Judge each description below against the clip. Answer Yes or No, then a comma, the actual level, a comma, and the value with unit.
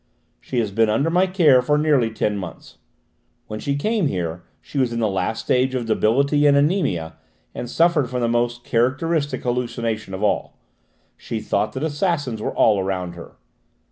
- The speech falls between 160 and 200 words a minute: Yes, average, 175 wpm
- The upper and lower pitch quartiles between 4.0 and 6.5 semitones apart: Yes, average, 5.1 semitones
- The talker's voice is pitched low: Yes, low, 120 Hz